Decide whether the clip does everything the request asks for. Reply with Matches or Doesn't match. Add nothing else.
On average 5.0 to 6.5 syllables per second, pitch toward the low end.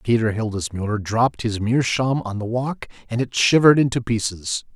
Matches